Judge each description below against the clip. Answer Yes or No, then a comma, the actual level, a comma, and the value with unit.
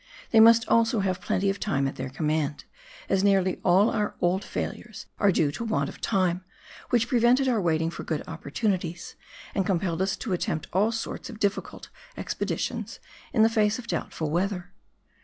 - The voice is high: Yes, high, 195 Hz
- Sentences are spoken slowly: No, average, 175 wpm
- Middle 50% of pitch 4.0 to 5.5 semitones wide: Yes, average, 4.5 semitones